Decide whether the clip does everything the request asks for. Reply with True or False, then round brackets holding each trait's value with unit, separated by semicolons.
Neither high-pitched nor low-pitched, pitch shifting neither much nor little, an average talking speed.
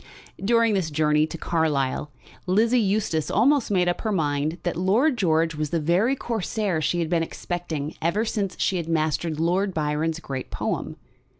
True (170 Hz; 4.5 semitones; 170 wpm)